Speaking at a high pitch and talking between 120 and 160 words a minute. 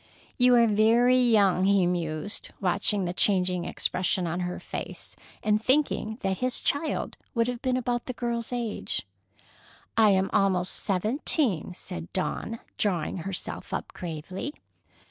Yes: high, 205 Hz; average, 140 wpm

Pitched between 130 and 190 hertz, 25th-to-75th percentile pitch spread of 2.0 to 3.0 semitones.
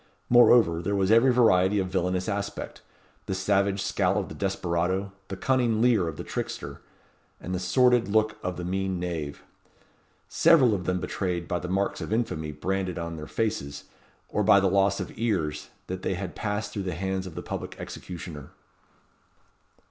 No: very low, 95 Hz; average, 2.7 semitones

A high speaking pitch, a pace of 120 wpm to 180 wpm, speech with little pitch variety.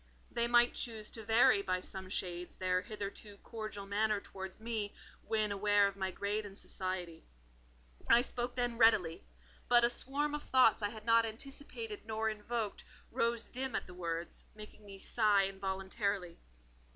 No: high, 210 Hz; average, 160 wpm; average, 3.2 semitones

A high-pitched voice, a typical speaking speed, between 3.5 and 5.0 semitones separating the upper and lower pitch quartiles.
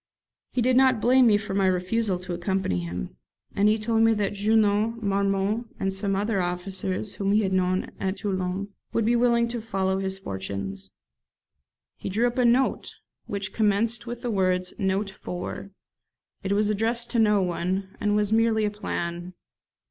No: high, 200 Hz; average, 180 wpm; average, 3.0 semitones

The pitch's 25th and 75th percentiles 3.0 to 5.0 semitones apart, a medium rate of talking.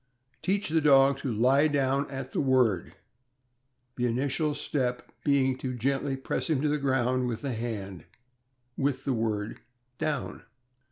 No: narrow, 2.5 semitones; average, 150 wpm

